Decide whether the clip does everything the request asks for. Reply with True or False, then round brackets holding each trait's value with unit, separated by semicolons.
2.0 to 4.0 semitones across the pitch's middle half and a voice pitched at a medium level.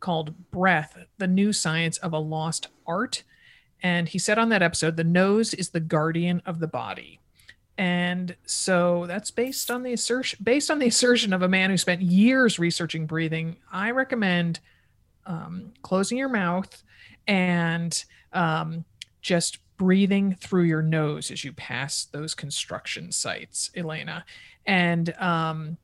True (3.2 semitones; 175 Hz)